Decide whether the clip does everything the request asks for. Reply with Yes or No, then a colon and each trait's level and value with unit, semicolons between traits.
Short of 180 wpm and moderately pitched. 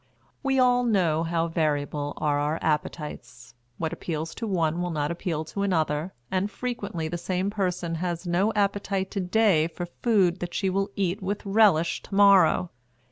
Yes: average, 170 wpm; medium, 175 Hz